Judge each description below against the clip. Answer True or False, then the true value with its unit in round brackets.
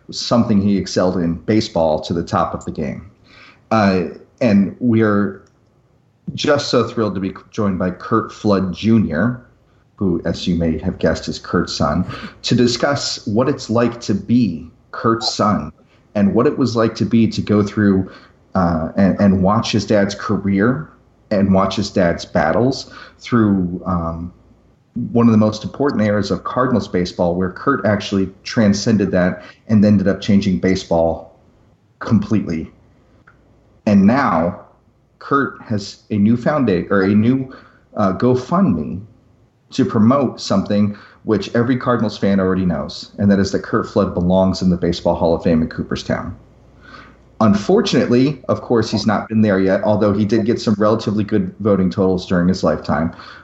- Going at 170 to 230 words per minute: False (160 wpm)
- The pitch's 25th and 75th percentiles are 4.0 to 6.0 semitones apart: False (3.5 semitones)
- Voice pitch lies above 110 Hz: False (105 Hz)